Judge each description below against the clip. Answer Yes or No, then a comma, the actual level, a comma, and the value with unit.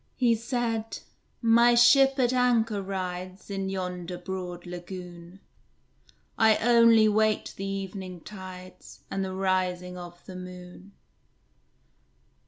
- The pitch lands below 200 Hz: Yes, high, 190 Hz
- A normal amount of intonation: Yes, average, 3.8 semitones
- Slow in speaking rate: Yes, slow, 110 wpm